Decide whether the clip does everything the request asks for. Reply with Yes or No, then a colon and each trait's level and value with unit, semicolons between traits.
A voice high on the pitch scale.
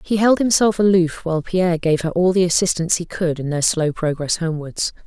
No: medium, 175 Hz